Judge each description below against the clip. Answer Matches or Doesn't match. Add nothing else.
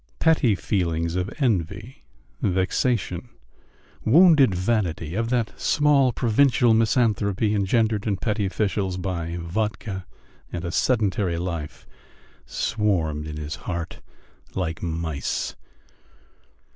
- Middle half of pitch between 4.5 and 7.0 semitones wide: Matches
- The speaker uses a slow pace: Matches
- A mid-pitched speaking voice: Doesn't match